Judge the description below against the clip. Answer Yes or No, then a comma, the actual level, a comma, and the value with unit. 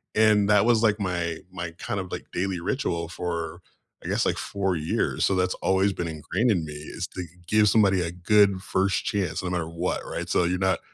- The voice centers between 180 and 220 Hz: No, very low, 95 Hz